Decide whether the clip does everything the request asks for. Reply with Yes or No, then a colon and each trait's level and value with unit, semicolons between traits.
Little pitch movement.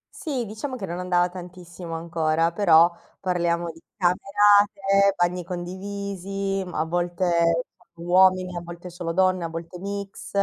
Yes: narrow, 2.3 semitones